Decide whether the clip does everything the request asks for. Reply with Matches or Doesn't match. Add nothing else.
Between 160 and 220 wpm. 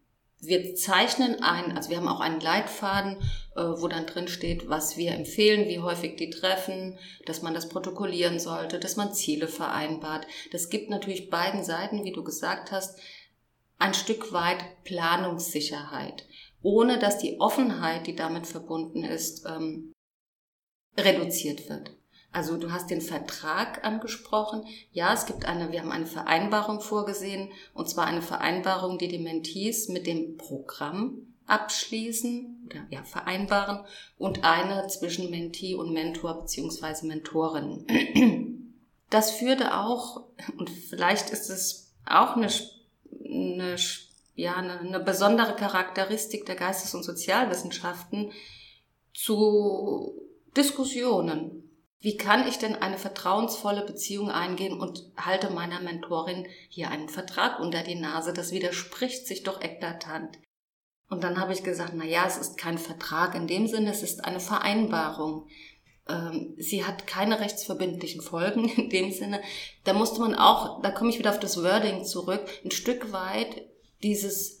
Doesn't match